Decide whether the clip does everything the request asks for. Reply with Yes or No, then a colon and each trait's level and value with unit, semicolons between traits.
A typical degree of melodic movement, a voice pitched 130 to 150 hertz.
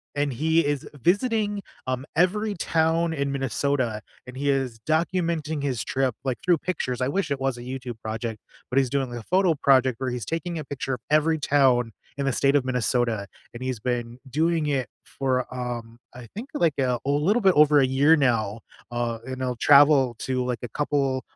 Yes: average, 4.0 semitones; low, 135 Hz